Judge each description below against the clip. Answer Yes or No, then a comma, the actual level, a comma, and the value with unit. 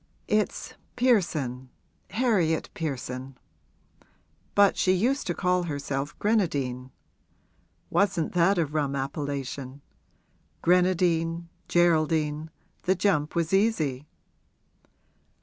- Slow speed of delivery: Yes, slow, 85 wpm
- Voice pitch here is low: No, medium, 165 Hz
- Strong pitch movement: No, average, 4.8 semitones